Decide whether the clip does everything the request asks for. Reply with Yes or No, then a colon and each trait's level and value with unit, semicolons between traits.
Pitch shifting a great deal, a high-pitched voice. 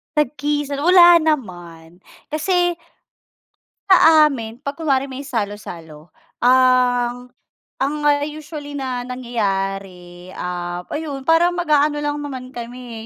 Yes: wide, 5.7 semitones; very high, 260 Hz